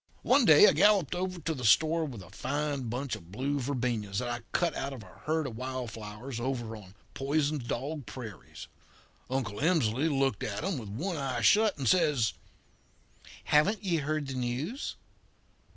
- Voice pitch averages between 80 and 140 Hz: Yes, low, 135 Hz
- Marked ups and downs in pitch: No, average, 4.8 semitones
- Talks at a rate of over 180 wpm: No, average, 175 wpm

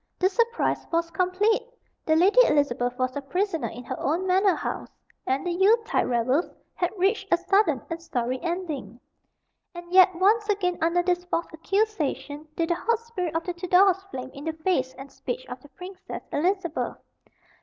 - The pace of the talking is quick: No, average, 175 wpm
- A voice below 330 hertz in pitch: No, very high, 350 Hz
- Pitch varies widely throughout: No, average, 4.5 semitones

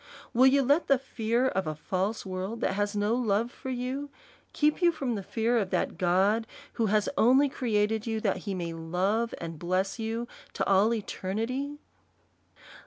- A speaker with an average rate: Yes, average, 175 wpm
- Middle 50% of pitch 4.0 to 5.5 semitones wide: Yes, average, 4.3 semitones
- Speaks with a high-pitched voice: Yes, high, 220 Hz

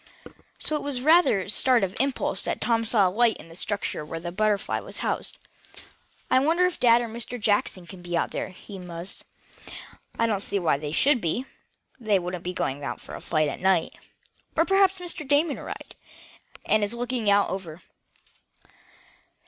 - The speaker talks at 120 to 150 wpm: No, average, 195 wpm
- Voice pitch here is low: No, high, 210 Hz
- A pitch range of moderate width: No, wide, 5.9 semitones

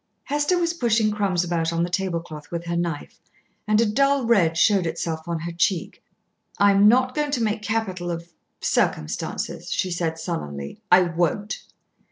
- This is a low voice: No, medium, 180 Hz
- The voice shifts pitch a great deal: No, average, 4.6 semitones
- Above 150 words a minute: Yes, average, 170 wpm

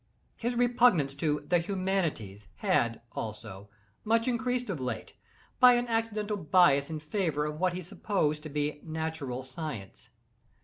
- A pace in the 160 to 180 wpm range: No, average, 140 wpm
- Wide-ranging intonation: Yes, wide, 6.7 semitones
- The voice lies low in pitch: No, medium, 160 Hz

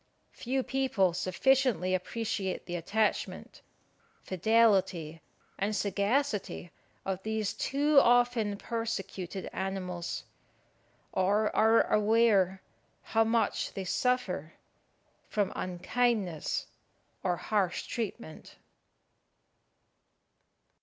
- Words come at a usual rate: No, slow, 80 wpm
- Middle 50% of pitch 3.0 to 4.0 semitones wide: Yes, average, 3.7 semitones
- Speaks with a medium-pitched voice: No, high, 205 Hz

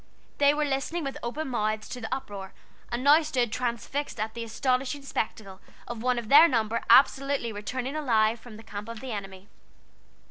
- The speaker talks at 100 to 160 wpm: No, average, 180 wpm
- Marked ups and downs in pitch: No, average, 4.0 semitones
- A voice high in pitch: Yes, high, 240 Hz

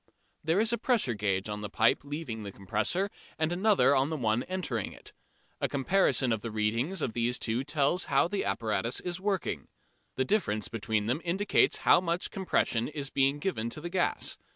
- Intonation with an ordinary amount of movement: No, wide, 8.0 semitones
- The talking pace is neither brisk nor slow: Yes, average, 190 wpm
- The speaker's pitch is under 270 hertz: Yes, medium, 140 Hz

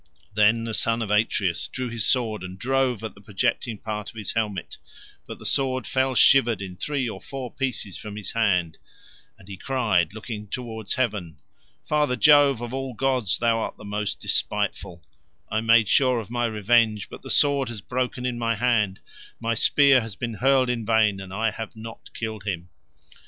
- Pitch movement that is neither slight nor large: Yes, average, 3.2 semitones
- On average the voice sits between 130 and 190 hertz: No, low, 115 Hz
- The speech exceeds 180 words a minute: Yes, average, 190 wpm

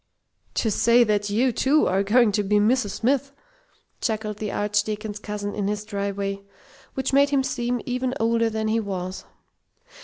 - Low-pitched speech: No, high, 215 Hz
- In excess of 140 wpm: Yes, average, 165 wpm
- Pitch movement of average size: Yes, average, 3.0 semitones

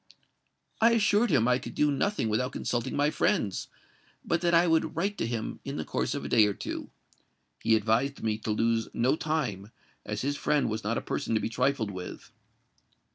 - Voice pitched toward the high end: No, low, 125 Hz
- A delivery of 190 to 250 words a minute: Yes, fast, 205 wpm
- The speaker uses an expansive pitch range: Yes, wide, 5.8 semitones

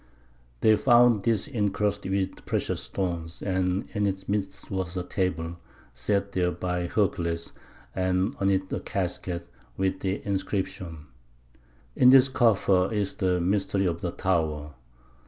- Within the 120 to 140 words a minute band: Yes, slow, 135 wpm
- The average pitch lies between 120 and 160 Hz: No, very low, 95 Hz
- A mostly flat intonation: Yes, narrow, 2.2 semitones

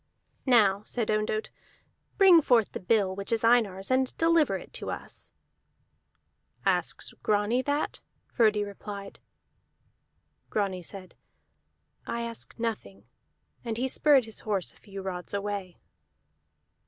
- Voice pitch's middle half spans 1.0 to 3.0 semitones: No, average, 3.5 semitones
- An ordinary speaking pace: No, slow, 120 wpm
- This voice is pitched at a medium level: No, high, 215 Hz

